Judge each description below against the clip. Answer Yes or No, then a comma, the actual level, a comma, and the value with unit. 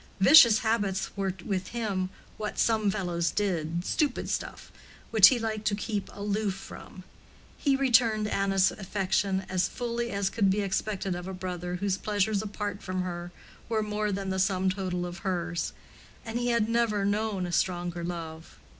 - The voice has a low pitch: No, high, 195 Hz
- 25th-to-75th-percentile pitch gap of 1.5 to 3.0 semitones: Yes, average, 2.7 semitones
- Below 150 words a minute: No, average, 165 wpm